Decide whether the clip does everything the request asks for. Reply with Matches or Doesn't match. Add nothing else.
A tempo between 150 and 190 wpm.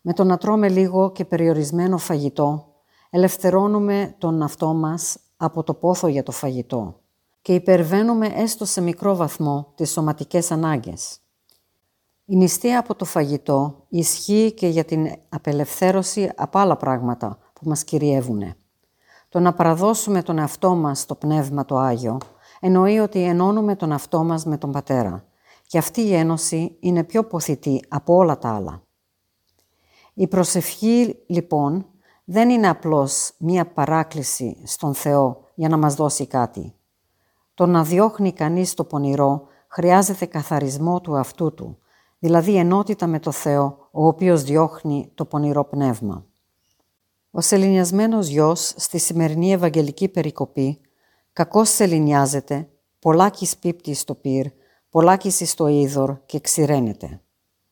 Doesn't match